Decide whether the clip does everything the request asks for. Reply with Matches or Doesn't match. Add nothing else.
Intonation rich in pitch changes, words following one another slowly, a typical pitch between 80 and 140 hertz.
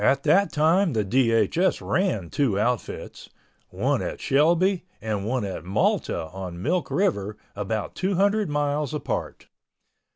Matches